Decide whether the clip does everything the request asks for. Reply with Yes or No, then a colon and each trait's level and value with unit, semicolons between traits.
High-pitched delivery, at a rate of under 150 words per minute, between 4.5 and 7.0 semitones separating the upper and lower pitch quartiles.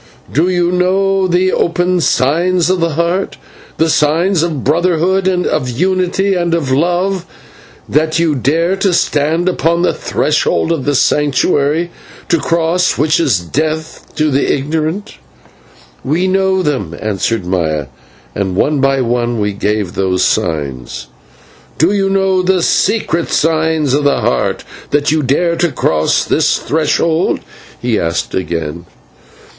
No: medium, 160 Hz; average, 140 wpm; average, 5.3 semitones